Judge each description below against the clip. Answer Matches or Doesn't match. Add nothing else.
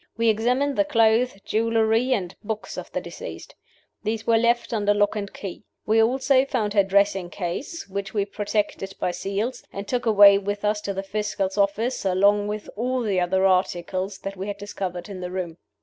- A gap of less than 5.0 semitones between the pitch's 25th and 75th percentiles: Matches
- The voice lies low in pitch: Doesn't match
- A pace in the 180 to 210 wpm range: Matches